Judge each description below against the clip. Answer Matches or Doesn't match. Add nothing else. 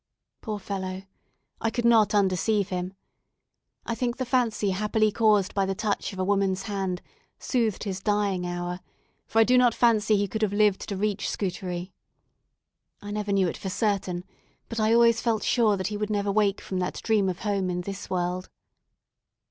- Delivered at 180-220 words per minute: Matches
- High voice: Matches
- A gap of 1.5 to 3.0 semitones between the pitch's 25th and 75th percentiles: Matches